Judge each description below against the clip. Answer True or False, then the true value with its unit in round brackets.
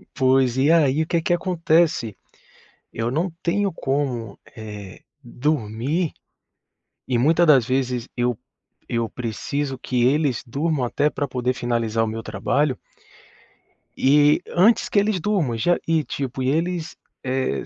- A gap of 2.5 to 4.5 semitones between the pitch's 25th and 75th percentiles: False (4.9 semitones)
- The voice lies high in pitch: False (135 Hz)